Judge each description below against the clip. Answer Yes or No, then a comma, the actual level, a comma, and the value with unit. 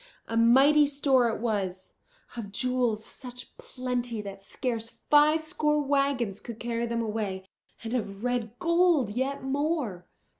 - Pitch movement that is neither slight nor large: Yes, average, 4.1 semitones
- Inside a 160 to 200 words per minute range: No, average, 140 wpm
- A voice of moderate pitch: No, high, 245 Hz